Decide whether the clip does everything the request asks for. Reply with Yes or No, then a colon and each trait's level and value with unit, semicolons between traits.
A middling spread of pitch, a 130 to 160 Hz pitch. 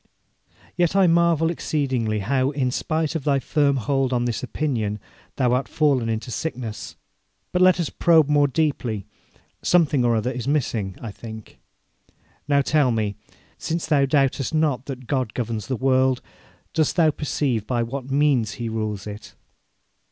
Yes: average, 4.4 semitones; low, 135 Hz